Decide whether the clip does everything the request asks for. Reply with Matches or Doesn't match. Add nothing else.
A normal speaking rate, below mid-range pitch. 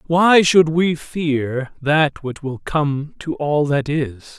Doesn't match